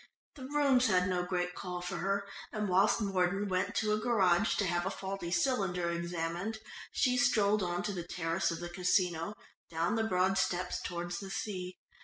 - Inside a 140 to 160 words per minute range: No, average, 185 wpm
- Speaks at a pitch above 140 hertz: Yes, medium, 185 Hz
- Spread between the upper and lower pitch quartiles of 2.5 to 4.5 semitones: Yes, average, 2.9 semitones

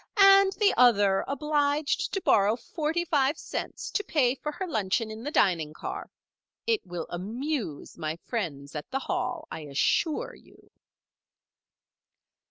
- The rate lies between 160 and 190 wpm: No, average, 140 wpm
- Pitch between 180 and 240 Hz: No, very high, 250 Hz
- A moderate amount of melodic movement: No, wide, 8.2 semitones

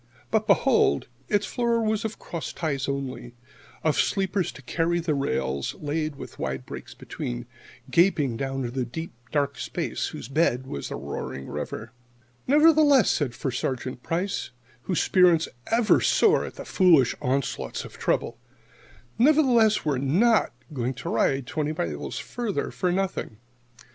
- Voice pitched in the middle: Yes, medium, 155 Hz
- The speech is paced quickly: No, average, 145 wpm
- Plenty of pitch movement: Yes, wide, 7.9 semitones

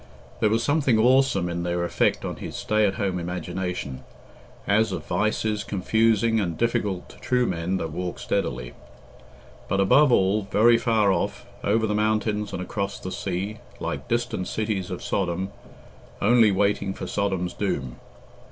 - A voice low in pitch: Yes, low, 100 Hz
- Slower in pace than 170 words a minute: Yes, average, 155 wpm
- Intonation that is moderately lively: Yes, average, 3.3 semitones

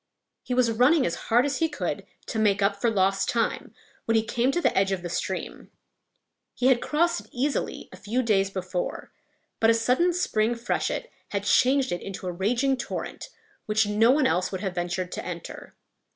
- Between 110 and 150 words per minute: No, average, 195 wpm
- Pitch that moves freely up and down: No, average, 4.7 semitones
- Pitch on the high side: Yes, high, 225 Hz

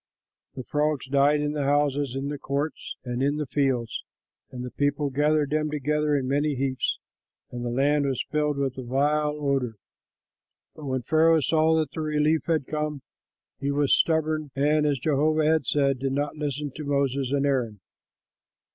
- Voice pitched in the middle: Yes, medium, 145 Hz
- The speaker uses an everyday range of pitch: No, narrow, 1.9 semitones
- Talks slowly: No, average, 175 wpm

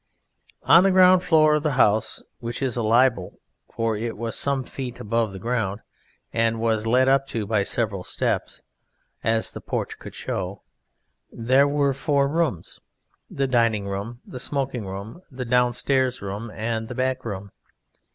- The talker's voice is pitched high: No, low, 120 Hz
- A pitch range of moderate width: Yes, average, 3.7 semitones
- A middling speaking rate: Yes, average, 160 wpm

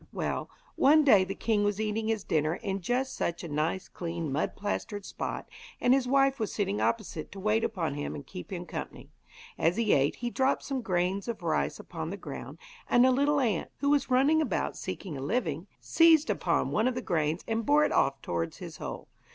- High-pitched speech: Yes, high, 210 Hz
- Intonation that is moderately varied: No, wide, 7.2 semitones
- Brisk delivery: Yes, fast, 210 wpm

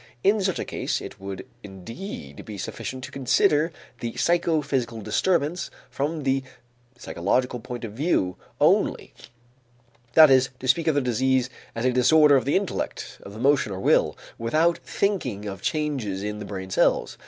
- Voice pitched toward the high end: No, low, 130 Hz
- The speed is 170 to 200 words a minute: No, average, 155 wpm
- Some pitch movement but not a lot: No, wide, 6.3 semitones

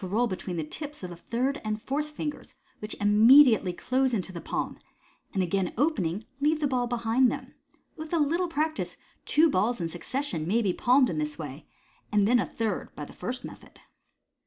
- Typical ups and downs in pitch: No, wide, 7.2 semitones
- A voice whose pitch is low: No, high, 230 Hz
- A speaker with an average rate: Yes, average, 195 wpm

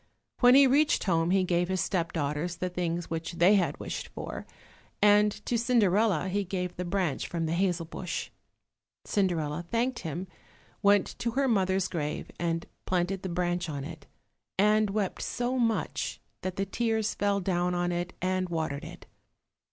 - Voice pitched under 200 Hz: Yes, medium, 185 Hz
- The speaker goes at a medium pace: Yes, average, 165 wpm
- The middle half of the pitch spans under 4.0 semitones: Yes, average, 3.1 semitones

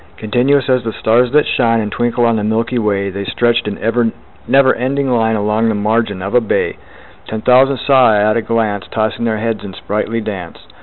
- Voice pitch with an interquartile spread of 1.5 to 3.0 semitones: Yes, narrow, 2.4 semitones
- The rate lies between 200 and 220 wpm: Yes, fast, 205 wpm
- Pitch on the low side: Yes, low, 115 Hz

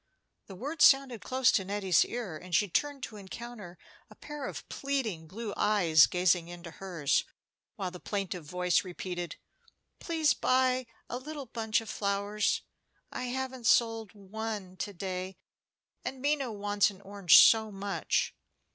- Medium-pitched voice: No, high, 205 Hz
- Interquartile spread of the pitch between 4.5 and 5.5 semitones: Yes, average, 5.2 semitones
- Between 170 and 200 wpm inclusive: No, average, 145 wpm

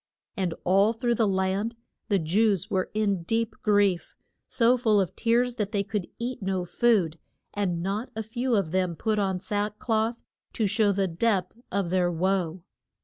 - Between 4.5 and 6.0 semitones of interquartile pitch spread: No, average, 3.1 semitones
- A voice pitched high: Yes, high, 200 Hz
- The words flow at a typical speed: Yes, average, 175 wpm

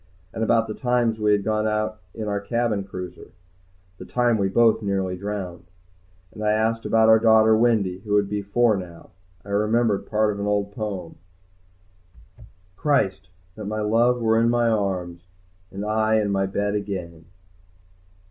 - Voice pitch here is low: Yes, low, 105 Hz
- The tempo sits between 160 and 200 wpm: Yes, average, 165 wpm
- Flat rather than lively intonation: Yes, narrow, 2.2 semitones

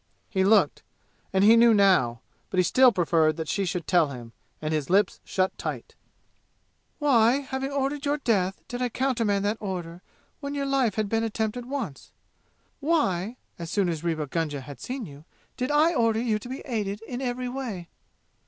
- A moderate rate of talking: Yes, average, 180 wpm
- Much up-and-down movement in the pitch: Yes, wide, 6.4 semitones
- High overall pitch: Yes, high, 215 Hz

